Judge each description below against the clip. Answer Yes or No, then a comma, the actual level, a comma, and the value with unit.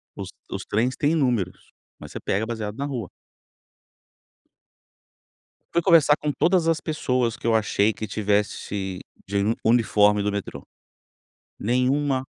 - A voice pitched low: Yes, low, 115 Hz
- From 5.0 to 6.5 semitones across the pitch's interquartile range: Yes, wide, 5.4 semitones